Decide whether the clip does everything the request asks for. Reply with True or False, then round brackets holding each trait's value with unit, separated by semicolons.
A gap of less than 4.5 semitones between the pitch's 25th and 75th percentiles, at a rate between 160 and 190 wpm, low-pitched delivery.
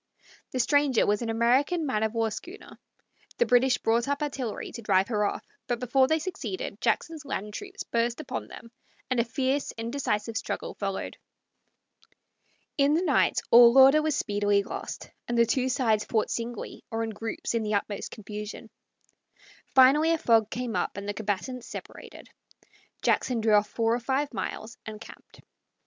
False (3.7 semitones; 170 wpm; 235 Hz)